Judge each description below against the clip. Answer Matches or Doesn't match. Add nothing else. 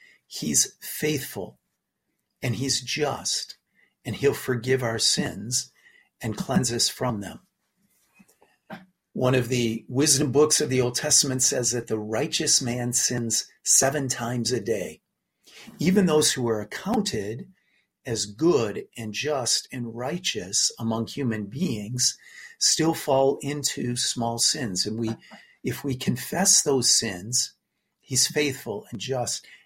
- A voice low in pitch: Matches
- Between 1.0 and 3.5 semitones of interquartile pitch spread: Doesn't match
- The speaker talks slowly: Matches